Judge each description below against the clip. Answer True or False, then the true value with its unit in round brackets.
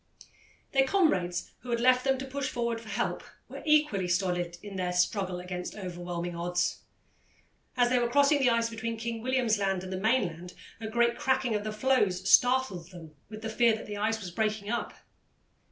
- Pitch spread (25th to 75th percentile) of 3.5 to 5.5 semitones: True (5.1 semitones)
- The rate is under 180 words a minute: False (190 wpm)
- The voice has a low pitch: False (220 Hz)